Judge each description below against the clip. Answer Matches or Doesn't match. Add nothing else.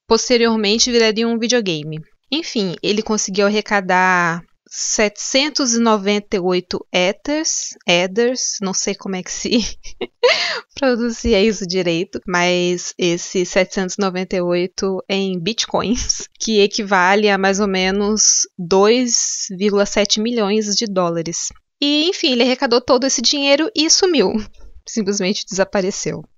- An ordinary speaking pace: Doesn't match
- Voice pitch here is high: Matches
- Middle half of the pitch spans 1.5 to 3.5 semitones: Doesn't match